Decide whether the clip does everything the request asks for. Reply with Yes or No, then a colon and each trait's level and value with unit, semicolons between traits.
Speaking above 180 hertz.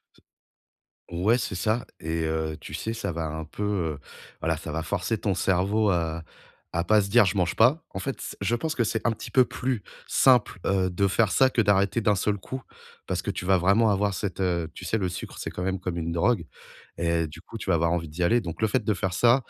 No: very low, 95 Hz